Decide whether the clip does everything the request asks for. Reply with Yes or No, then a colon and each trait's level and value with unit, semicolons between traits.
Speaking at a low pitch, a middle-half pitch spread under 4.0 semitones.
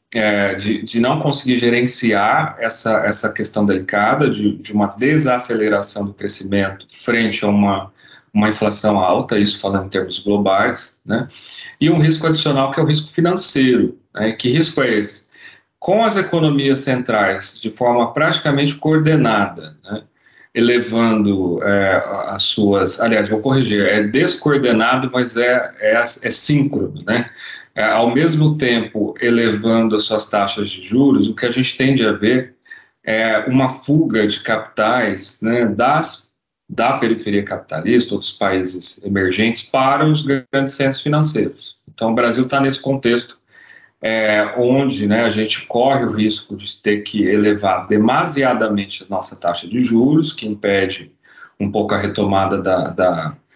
No: low, 115 Hz; average, 4.6 semitones